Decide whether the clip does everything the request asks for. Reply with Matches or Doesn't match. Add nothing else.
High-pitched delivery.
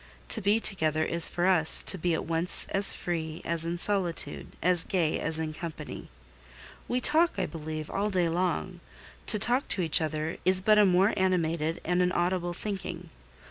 Doesn't match